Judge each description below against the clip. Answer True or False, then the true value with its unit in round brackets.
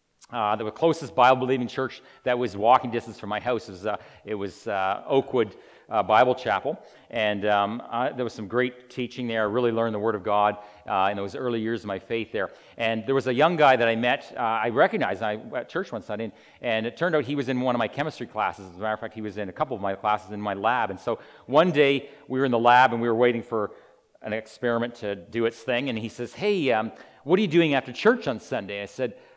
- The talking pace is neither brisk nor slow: False (260 wpm)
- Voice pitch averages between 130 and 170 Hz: False (115 Hz)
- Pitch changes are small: False (3.1 semitones)